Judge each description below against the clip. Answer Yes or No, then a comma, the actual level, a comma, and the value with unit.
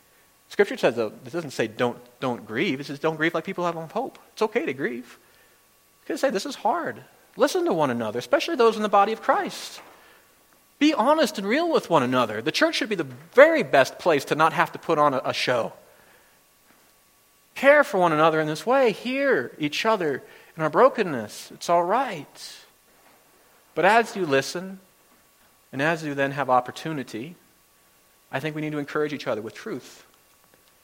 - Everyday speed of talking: Yes, average, 195 wpm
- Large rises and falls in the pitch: Yes, wide, 7.9 semitones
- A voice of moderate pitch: Yes, medium, 170 Hz